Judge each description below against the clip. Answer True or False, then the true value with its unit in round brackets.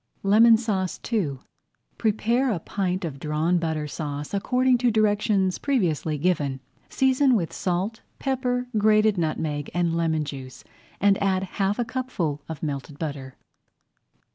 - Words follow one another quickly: False (135 wpm)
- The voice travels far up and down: True (6.2 semitones)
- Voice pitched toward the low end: False (185 Hz)